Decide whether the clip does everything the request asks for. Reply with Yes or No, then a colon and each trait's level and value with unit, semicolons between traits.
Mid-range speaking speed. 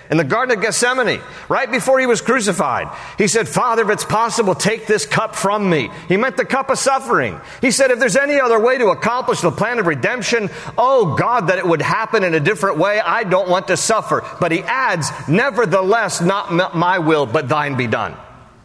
No: fast, 210 wpm